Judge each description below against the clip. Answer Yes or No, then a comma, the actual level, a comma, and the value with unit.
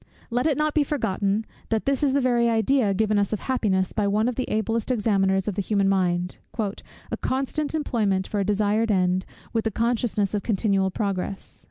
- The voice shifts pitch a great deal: No, average, 3.6 semitones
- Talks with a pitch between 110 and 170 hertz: No, high, 215 Hz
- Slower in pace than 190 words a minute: No, average, 195 wpm